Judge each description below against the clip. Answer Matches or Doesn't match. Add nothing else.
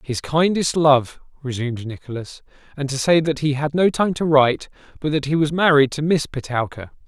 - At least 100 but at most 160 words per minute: Doesn't match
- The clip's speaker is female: Doesn't match